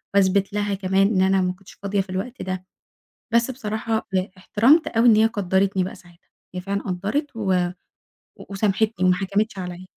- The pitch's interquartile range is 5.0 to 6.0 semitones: No, narrow, 2.6 semitones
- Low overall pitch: No, high, 195 Hz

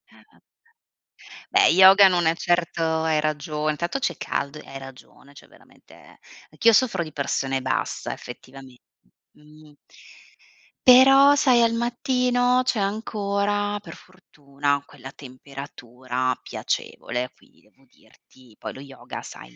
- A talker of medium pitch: Yes, medium, 155 Hz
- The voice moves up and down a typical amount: No, wide, 7.1 semitones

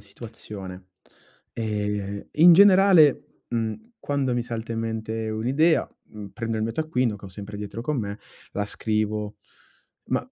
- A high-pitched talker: No, low, 110 Hz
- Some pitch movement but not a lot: Yes, average, 3.5 semitones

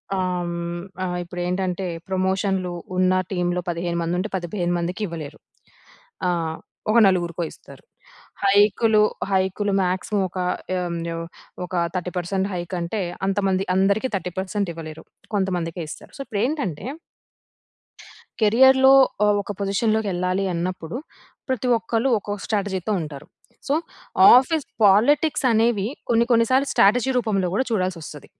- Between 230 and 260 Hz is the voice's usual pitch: No, high, 190 Hz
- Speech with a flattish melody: No, average, 3.3 semitones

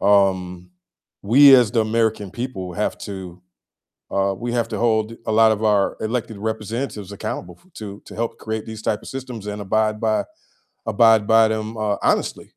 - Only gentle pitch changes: Yes, narrow, 1.9 semitones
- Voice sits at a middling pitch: No, low, 110 Hz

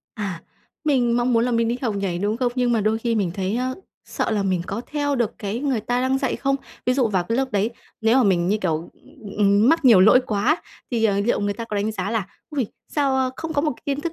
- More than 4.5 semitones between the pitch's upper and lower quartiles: No, average, 4.2 semitones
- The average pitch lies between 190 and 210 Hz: No, high, 230 Hz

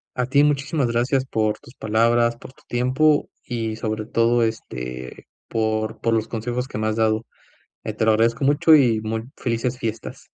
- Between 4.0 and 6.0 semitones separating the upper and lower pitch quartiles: No, narrow, 2.4 semitones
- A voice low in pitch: Yes, low, 115 Hz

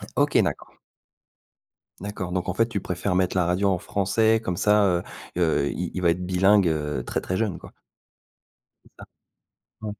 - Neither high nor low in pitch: No, very low, 90 Hz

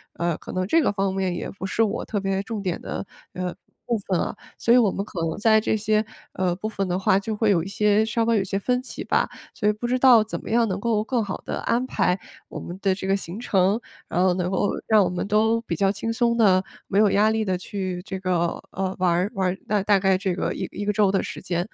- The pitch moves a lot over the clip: No, average, 2.7 semitones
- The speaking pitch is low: No, high, 200 Hz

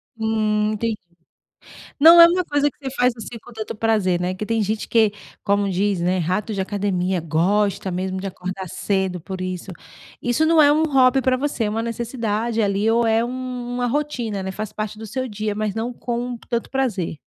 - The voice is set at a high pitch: Yes, high, 215 Hz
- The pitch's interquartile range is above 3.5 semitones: Yes, average, 3.9 semitones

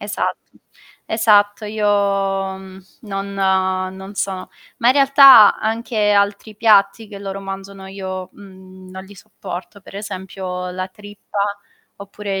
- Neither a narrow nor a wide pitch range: No, narrow, 1.6 semitones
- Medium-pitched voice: No, high, 195 Hz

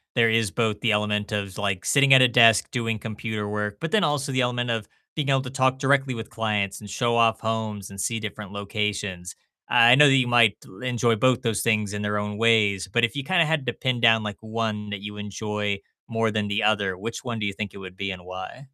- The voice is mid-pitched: No, low, 110 Hz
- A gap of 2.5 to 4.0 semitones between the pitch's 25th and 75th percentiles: Yes, average, 2.8 semitones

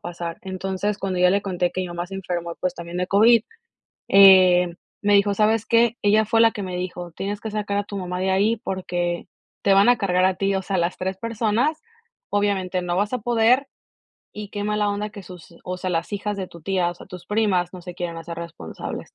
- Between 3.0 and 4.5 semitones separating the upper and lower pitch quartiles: No, narrow, 2.6 semitones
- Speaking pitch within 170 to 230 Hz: Yes, high, 190 Hz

